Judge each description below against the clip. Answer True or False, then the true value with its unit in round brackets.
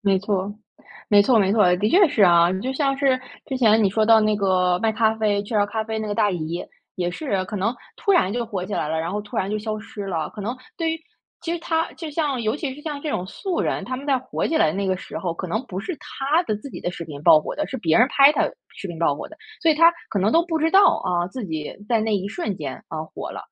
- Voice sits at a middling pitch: False (215 Hz)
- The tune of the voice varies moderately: False (6.5 semitones)